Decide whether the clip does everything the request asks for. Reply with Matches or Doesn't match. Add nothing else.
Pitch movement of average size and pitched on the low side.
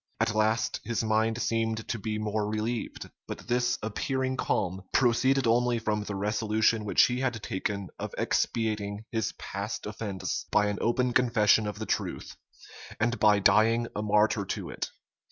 Doesn't match